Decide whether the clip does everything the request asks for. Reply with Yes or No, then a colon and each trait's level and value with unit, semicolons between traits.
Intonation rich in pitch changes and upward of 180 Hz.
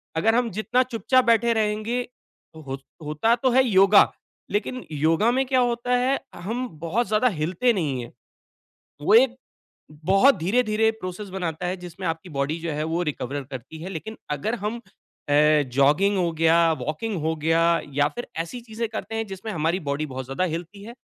Yes: wide, 6.3 semitones; high, 190 Hz